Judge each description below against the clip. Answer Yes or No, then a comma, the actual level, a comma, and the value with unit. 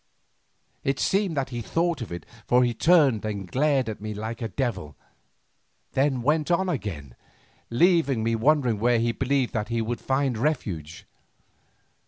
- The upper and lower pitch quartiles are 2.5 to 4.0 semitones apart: No, average, 4.6 semitones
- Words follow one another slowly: No, average, 160 wpm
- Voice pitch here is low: Yes, low, 120 Hz